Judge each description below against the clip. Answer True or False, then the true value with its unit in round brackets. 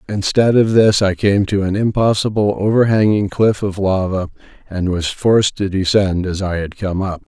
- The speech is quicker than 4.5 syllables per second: True (4.8 syllables/s)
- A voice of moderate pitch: False (100 Hz)